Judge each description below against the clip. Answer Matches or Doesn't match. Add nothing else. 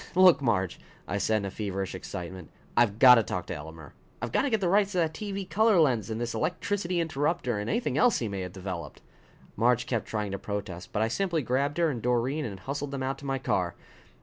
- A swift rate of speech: Matches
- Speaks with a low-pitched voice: Matches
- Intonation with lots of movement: Matches